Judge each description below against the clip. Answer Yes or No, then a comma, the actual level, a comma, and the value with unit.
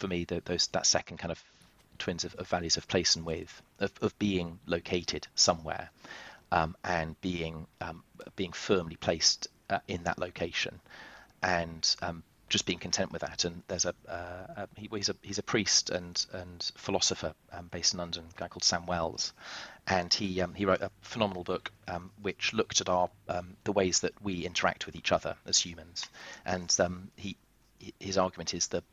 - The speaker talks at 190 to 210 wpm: Yes, average, 195 wpm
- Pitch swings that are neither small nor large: No, narrow, 1.9 semitones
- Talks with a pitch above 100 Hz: No, very low, 90 Hz